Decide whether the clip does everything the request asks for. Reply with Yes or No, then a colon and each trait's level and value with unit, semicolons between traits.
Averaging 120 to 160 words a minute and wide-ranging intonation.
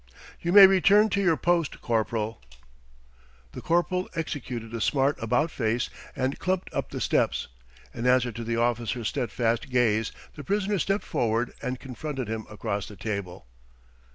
Yes: average, 155 wpm; wide, 6.8 semitones